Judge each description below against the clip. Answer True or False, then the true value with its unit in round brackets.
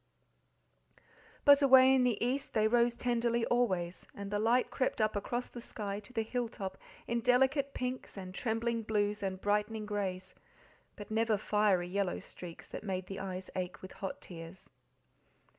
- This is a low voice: False (215 Hz)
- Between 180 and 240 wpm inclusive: False (165 wpm)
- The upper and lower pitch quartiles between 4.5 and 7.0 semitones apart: False (3.8 semitones)